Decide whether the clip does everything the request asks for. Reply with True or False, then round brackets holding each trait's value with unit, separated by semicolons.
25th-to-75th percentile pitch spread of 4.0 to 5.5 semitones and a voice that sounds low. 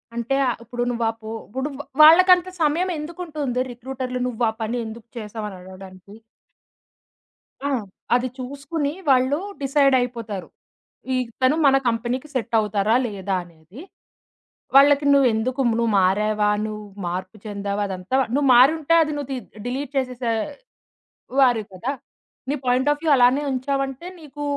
False (4.4 semitones; 250 Hz)